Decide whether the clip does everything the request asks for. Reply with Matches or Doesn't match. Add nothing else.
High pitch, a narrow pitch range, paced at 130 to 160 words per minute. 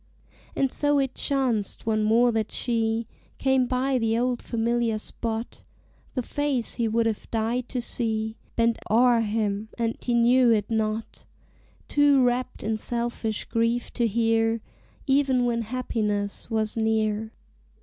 Matches